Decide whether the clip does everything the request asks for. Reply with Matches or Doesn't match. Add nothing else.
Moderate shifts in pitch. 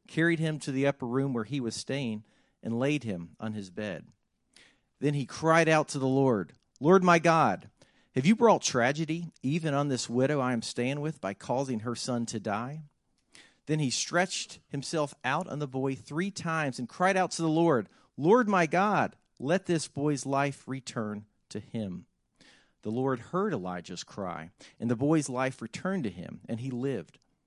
Matches